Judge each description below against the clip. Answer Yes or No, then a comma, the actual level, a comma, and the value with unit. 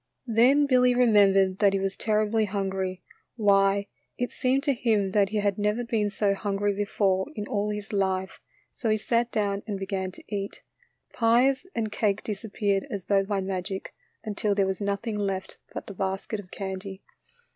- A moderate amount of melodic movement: No, narrow, 2.0 semitones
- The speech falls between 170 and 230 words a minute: Yes, average, 175 wpm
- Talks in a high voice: Yes, high, 205 Hz